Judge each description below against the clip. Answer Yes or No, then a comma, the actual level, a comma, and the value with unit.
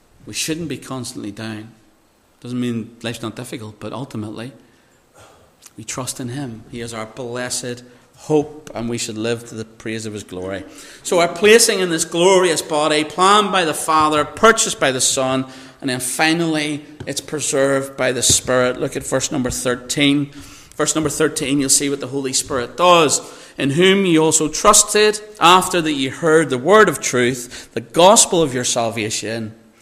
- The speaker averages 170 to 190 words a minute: Yes, average, 175 wpm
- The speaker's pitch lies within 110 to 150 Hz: Yes, low, 135 Hz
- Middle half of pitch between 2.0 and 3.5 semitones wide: No, average, 4.5 semitones